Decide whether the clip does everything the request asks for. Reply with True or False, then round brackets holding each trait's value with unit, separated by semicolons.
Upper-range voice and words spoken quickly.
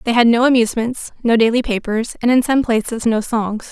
True (230 Hz; 210 wpm)